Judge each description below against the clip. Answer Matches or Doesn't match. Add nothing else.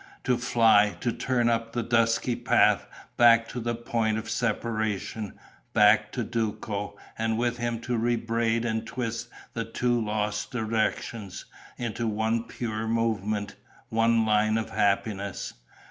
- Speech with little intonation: Matches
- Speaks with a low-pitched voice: Matches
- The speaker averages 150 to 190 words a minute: Doesn't match